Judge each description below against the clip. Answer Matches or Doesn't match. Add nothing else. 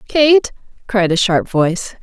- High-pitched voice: Matches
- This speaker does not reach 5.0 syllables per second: Matches